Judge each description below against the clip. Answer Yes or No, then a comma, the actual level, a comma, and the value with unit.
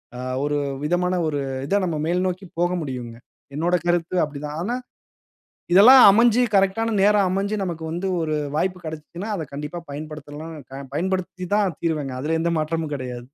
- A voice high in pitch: No, medium, 170 Hz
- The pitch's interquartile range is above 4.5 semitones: No, average, 3.8 semitones